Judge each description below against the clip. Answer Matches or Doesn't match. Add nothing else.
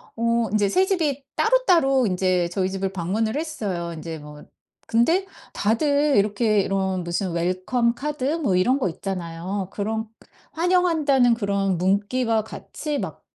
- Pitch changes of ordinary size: Doesn't match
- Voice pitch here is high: Matches